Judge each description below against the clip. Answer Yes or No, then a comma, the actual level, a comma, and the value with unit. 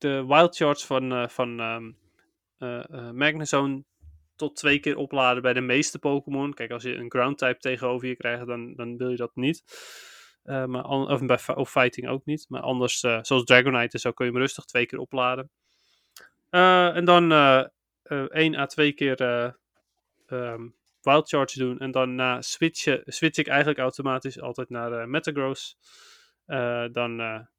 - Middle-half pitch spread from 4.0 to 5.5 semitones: No, narrow, 2.6 semitones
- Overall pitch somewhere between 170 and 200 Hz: No, low, 130 Hz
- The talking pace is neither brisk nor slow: Yes, average, 175 wpm